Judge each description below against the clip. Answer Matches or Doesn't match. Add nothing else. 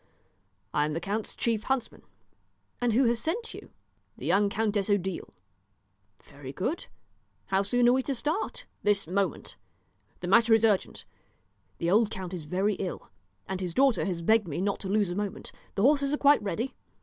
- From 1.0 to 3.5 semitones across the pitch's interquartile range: Doesn't match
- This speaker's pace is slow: Doesn't match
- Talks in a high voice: Matches